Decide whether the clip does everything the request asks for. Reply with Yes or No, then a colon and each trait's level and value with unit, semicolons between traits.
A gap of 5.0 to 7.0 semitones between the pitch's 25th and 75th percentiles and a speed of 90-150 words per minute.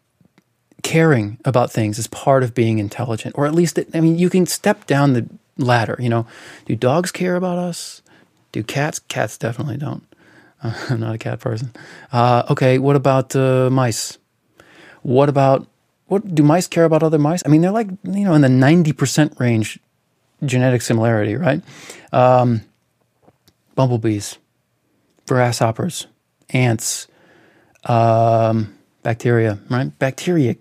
Yes: average, 5.3 semitones; average, 145 wpm